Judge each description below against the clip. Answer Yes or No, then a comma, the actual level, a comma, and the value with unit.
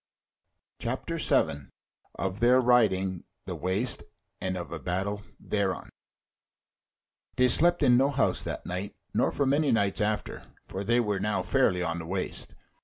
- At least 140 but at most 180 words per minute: Yes, average, 150 wpm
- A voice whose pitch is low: Yes, low, 100 Hz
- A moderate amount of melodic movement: Yes, average, 4.8 semitones